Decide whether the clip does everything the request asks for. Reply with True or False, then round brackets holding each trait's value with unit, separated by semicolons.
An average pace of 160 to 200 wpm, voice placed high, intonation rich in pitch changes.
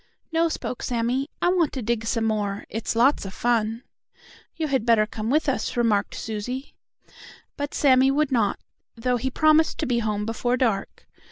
False (175 wpm; 240 Hz; 3.6 semitones)